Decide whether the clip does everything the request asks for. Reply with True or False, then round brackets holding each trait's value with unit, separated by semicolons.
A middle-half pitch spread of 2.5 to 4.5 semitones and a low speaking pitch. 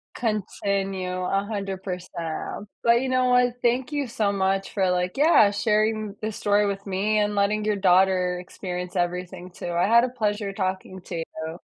False (2.8 semitones; 200 Hz)